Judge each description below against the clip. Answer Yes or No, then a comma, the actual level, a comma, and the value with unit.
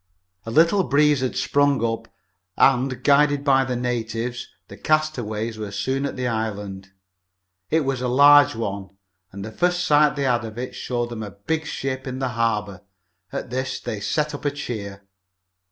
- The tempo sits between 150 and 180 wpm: Yes, average, 175 wpm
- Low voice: Yes, low, 125 Hz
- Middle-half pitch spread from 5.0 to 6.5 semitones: No, average, 4.3 semitones